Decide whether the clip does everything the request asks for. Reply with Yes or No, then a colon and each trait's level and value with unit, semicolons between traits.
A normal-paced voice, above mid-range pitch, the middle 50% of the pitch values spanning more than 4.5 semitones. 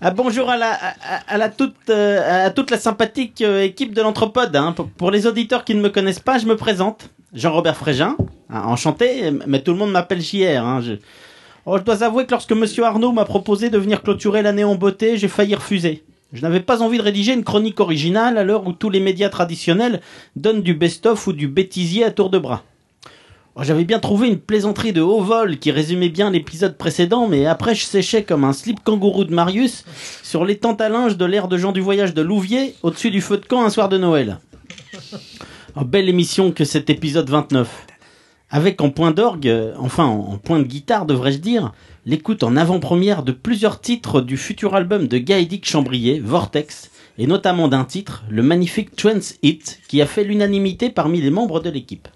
Yes: average, 210 wpm; high, 195 Hz; wide, 5.6 semitones